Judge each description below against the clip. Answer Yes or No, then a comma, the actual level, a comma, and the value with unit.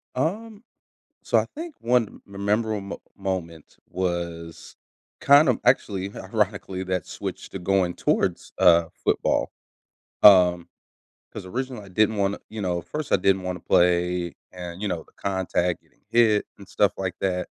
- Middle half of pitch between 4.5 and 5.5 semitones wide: No, average, 3.3 semitones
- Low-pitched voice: Yes, very low, 95 Hz